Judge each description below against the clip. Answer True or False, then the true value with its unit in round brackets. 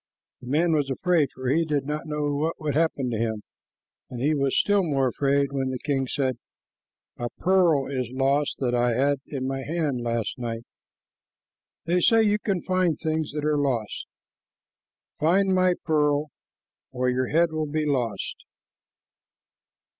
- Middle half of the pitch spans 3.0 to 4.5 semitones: True (3.6 semitones)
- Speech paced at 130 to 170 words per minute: True (160 wpm)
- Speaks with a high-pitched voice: False (145 Hz)